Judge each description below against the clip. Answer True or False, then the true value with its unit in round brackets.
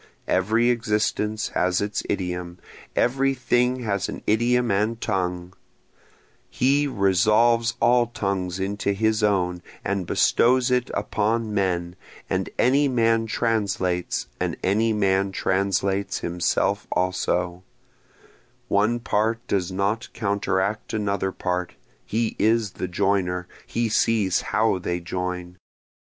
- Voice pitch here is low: True (100 Hz)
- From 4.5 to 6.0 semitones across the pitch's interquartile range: False (3.7 semitones)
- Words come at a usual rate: False (115 wpm)